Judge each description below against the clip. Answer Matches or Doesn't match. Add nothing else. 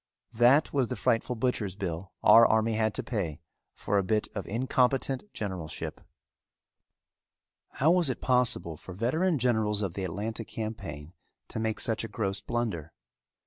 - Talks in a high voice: Doesn't match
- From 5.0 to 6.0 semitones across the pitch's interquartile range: Doesn't match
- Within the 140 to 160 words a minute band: Matches